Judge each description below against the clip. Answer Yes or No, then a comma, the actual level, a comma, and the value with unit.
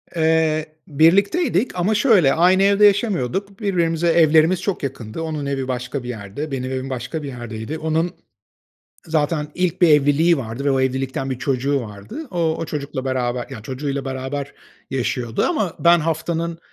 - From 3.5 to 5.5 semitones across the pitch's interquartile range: Yes, average, 4.5 semitones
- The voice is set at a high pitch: No, medium, 150 Hz